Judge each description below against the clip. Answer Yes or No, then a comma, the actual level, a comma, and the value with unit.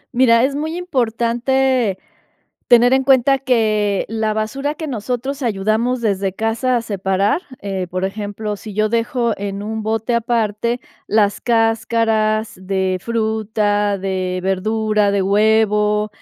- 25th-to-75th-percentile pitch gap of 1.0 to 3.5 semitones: Yes, average, 2.7 semitones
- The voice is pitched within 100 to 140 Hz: No, high, 220 Hz